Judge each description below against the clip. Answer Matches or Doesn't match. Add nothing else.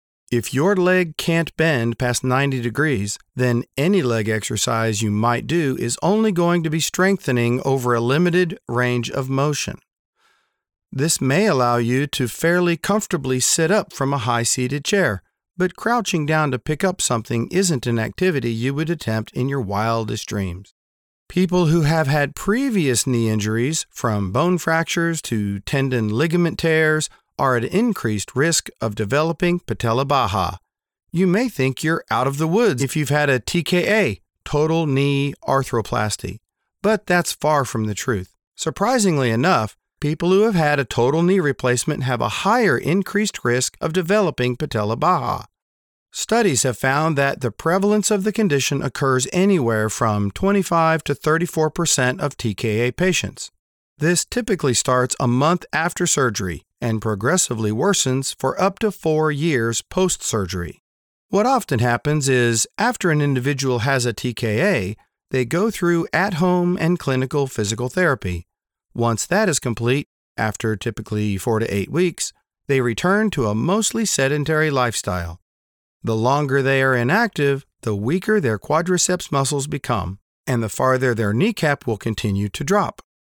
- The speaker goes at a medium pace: Matches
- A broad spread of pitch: Matches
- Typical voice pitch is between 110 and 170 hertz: Matches